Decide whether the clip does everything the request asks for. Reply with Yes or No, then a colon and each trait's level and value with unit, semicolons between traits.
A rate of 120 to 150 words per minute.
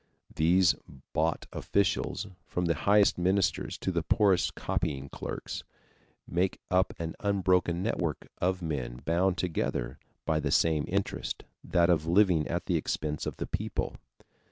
Yes: average, 140 wpm